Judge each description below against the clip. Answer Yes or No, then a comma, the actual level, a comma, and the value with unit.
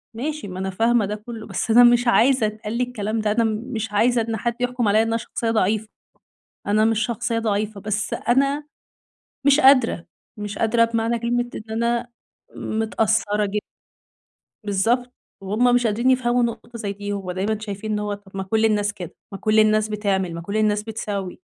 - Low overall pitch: No, high, 220 Hz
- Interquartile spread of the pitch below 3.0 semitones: Yes, narrow, 2.4 semitones